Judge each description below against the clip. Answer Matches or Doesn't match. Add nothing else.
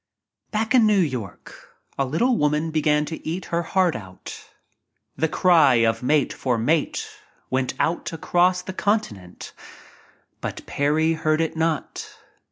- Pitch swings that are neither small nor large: Matches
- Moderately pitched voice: Matches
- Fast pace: Doesn't match